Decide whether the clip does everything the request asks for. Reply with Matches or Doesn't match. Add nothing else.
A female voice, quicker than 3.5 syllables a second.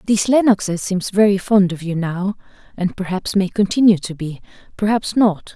Matches